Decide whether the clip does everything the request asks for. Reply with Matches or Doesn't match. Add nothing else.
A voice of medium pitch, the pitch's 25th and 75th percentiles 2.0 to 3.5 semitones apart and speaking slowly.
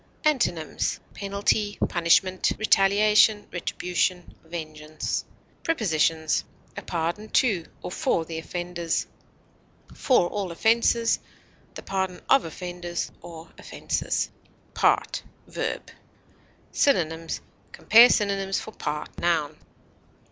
Doesn't match